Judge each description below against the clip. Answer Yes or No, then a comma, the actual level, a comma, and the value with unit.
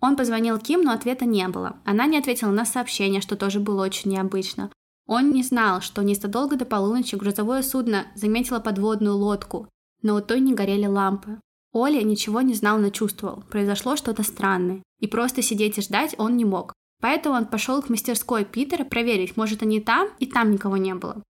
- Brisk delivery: Yes, fast, 190 wpm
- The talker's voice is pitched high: Yes, high, 220 Hz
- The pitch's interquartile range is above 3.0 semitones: Yes, average, 3.4 semitones